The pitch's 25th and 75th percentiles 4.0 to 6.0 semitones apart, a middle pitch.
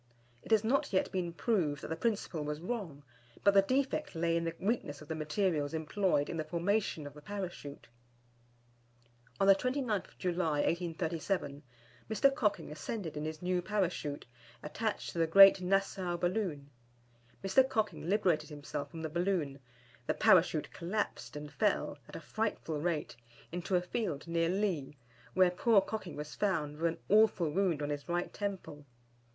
Yes: average, 4.7 semitones; medium, 175 Hz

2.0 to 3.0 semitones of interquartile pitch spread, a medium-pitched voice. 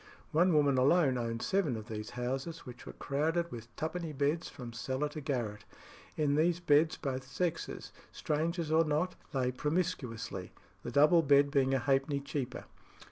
No: average, 4.0 semitones; medium, 145 Hz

